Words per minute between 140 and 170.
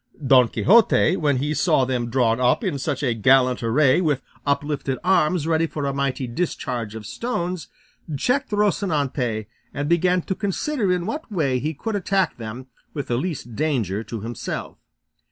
Yes: average, 165 wpm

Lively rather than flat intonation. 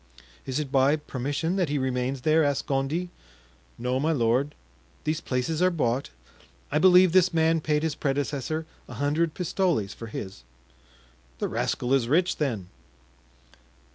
No: average, 4.0 semitones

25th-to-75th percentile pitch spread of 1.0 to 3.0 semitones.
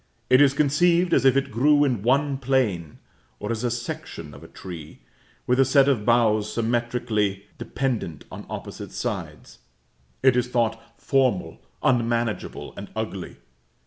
No: average, 3.9 semitones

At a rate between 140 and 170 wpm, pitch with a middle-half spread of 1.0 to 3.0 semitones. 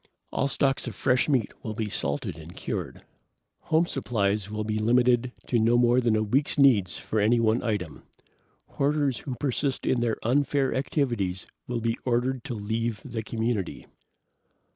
No: average, 165 wpm; average, 3.4 semitones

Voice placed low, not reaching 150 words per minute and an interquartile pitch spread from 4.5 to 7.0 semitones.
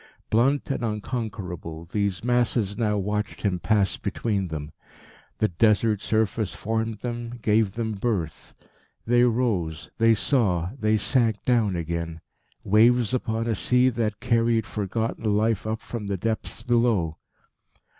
No: low, 110 Hz; slow, 135 wpm; average, 3.0 semitones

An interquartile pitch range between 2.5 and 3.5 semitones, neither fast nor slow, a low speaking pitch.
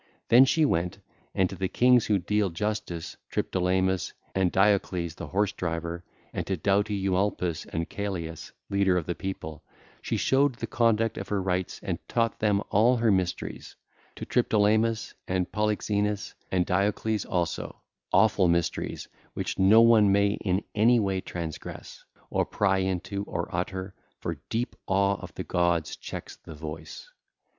Yes: average, 2.9 semitones; average, 150 wpm; very low, 95 Hz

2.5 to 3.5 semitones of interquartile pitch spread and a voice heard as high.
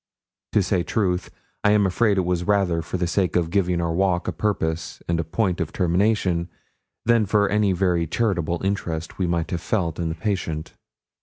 No: average, 3.0 semitones; very low, 90 Hz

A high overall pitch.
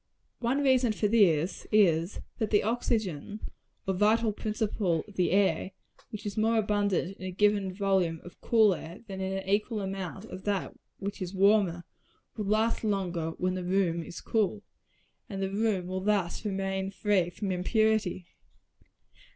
Yes: high, 195 Hz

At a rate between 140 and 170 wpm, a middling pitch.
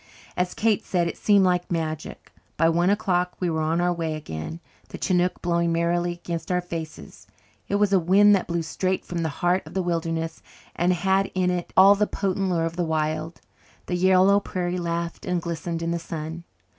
No: average, 200 wpm; medium, 175 Hz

